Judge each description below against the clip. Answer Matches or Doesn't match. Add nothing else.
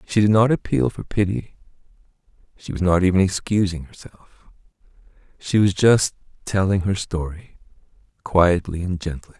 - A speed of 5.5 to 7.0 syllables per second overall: Doesn't match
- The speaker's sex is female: Doesn't match